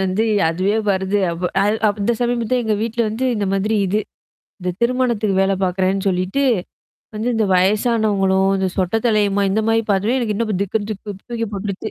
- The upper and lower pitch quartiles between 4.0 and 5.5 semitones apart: No, average, 2.8 semitones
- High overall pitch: Yes, high, 205 Hz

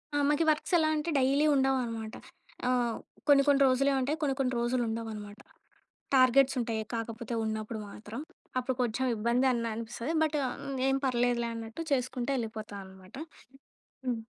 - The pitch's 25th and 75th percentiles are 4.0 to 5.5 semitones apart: No, average, 3.2 semitones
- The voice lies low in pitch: No, high, 245 Hz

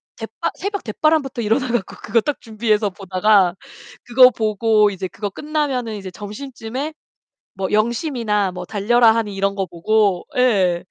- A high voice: Yes, high, 215 Hz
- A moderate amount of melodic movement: Yes, average, 3.7 semitones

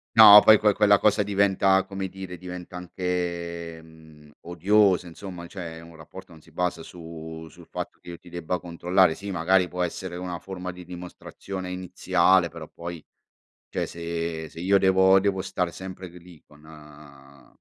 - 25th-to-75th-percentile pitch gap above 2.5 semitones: No, narrow, 2.2 semitones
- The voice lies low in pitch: Yes, very low, 90 Hz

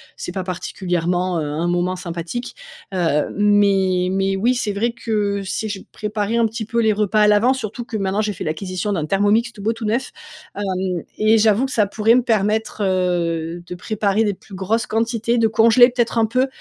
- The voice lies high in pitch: Yes, high, 205 Hz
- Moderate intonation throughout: Yes, average, 3.3 semitones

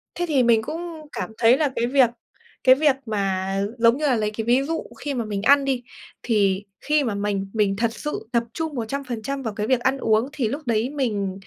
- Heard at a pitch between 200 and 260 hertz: Yes, high, 240 Hz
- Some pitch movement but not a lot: Yes, average, 4.5 semitones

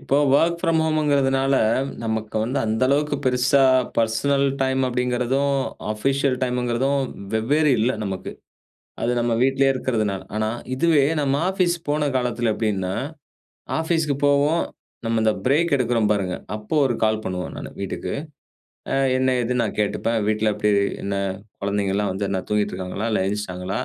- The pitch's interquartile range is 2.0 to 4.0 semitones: No, average, 4.5 semitones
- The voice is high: No, low, 125 Hz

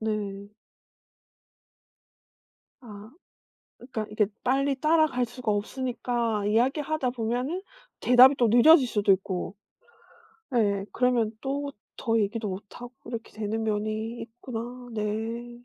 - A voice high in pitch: Yes, high, 230 Hz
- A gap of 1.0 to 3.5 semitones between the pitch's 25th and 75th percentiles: Yes, average, 2.9 semitones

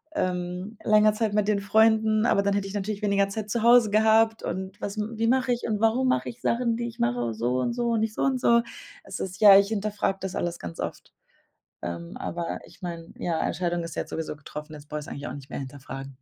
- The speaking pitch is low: No, high, 200 Hz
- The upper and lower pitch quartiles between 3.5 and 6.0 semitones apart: Yes, average, 4.8 semitones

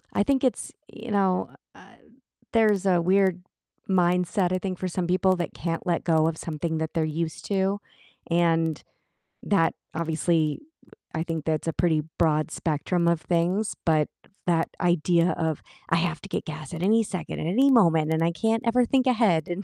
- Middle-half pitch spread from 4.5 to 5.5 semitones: No, average, 3.0 semitones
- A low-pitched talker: No, medium, 175 Hz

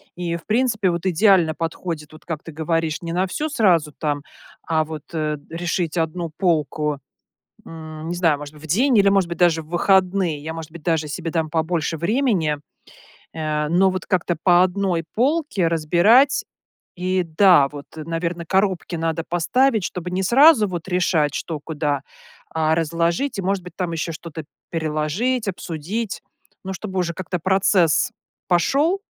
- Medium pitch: Yes, medium, 170 Hz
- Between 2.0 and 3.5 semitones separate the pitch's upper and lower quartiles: Yes, average, 3.1 semitones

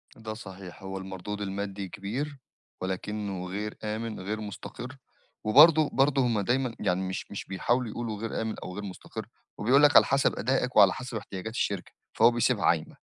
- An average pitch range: Yes, average, 4.0 semitones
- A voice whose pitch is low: Yes, low, 105 Hz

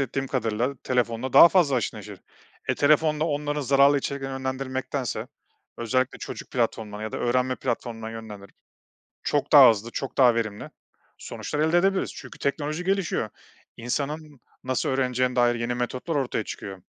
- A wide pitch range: No, average, 3.4 semitones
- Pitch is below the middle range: Yes, low, 130 Hz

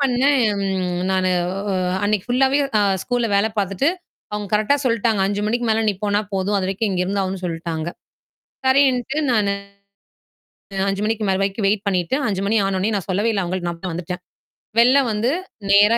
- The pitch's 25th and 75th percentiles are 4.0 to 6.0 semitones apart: No, average, 3.6 semitones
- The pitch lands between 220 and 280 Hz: No, high, 205 Hz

